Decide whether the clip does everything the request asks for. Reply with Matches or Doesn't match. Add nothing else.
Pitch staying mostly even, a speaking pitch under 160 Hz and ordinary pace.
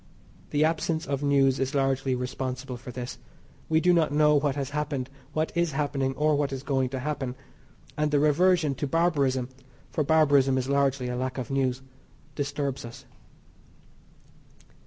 Matches